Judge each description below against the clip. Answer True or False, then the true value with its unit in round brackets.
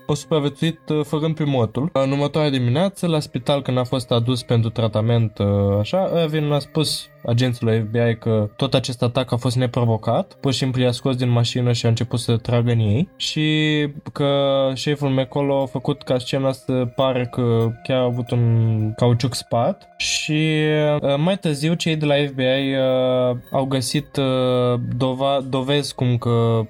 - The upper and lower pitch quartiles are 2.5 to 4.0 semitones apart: True (3.3 semitones)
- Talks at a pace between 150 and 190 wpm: True (160 wpm)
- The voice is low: True (130 Hz)